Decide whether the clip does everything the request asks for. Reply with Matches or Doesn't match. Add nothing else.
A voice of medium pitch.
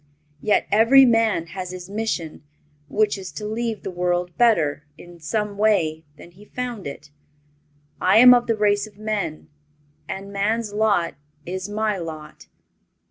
Doesn't match